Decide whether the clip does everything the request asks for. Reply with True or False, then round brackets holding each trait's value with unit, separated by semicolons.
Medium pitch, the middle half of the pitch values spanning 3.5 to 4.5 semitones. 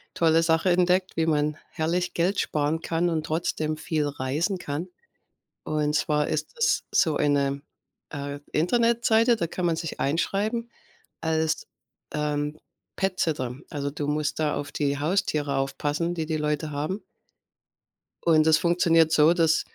False (160 Hz; 2.6 semitones)